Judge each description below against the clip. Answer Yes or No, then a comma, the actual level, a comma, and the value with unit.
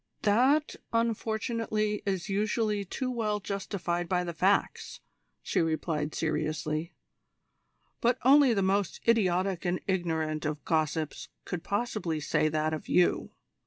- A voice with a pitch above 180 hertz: Yes, high, 190 Hz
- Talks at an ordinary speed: No, slow, 125 wpm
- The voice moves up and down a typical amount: Yes, average, 5.0 semitones